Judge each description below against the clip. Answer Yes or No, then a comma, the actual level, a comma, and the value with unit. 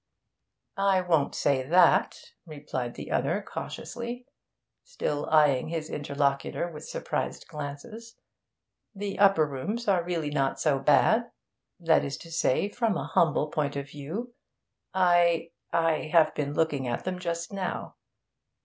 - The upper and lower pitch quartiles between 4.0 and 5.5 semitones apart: Yes, average, 4.5 semitones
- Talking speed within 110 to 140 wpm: Yes, slow, 135 wpm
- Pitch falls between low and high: Yes, medium, 160 Hz